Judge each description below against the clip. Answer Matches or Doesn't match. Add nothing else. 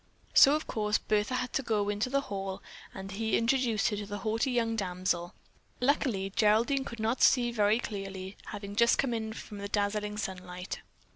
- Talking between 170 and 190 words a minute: Matches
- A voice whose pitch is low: Doesn't match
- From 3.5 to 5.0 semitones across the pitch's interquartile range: Doesn't match